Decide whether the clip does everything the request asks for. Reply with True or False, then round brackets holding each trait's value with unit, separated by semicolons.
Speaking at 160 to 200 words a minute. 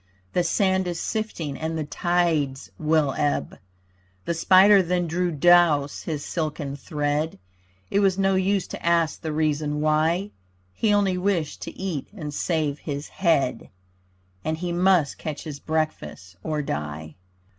False (145 wpm)